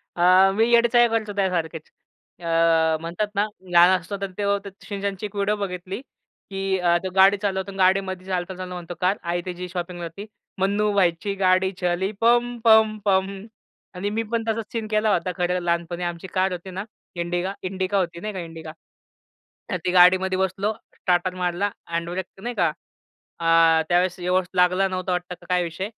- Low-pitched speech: No, medium, 185 Hz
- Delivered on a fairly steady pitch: Yes, narrow, 2.1 semitones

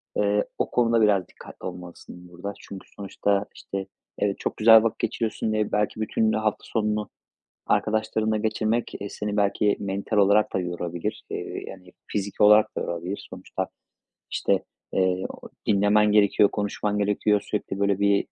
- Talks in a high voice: No, low, 105 Hz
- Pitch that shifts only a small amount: Yes, narrow, 1.6 semitones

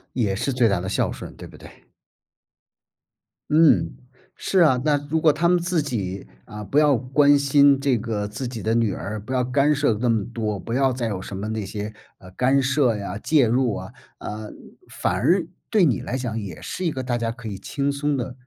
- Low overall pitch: Yes, low, 125 Hz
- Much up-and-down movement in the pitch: No, average, 4.9 semitones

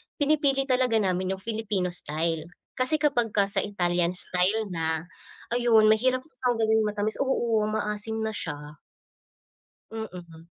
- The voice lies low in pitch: No, high, 215 Hz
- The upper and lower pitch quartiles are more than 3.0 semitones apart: Yes, average, 4.9 semitones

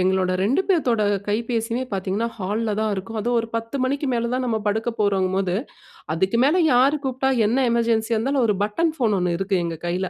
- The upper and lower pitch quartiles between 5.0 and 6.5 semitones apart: No, average, 4.2 semitones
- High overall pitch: Yes, high, 225 Hz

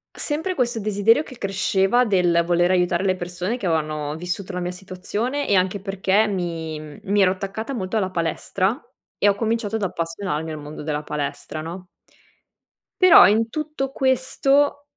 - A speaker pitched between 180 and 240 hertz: Yes, high, 190 Hz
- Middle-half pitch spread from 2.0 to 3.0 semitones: No, average, 4.5 semitones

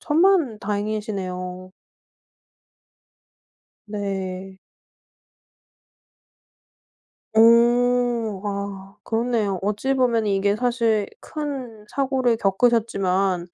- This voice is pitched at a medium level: No, high, 215 Hz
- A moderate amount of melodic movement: Yes, average, 3.8 semitones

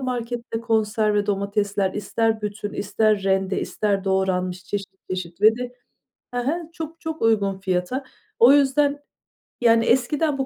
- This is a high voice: Yes, high, 215 Hz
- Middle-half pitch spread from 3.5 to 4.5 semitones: Yes, average, 3.9 semitones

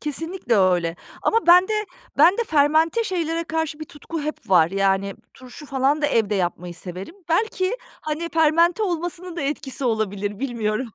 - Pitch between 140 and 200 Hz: No, very high, 295 Hz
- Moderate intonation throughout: No, wide, 8.1 semitones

